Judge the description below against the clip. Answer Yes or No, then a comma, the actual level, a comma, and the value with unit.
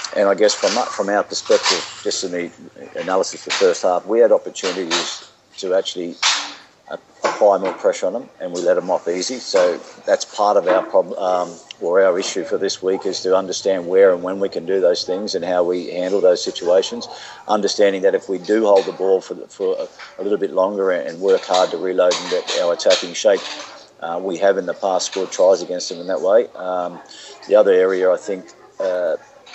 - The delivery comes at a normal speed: No, fast, 215 wpm